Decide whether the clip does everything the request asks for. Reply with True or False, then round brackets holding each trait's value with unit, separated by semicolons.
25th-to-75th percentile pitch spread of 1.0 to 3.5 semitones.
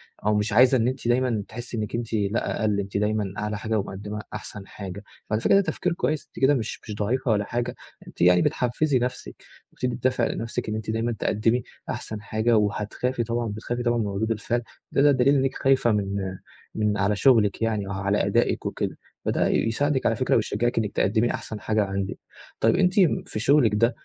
True (2.8 semitones)